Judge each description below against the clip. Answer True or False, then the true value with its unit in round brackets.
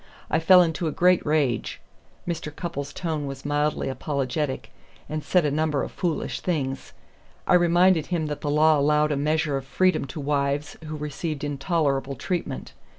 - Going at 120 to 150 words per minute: False (165 wpm)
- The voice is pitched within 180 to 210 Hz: False (150 Hz)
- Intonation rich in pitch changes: False (2.7 semitones)